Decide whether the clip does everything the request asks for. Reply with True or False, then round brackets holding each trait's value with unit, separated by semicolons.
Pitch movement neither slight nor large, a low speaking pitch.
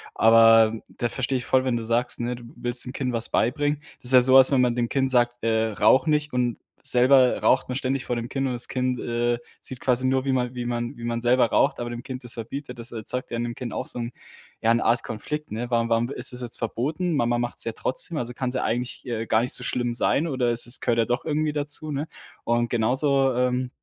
False (1.9 semitones; 125 Hz)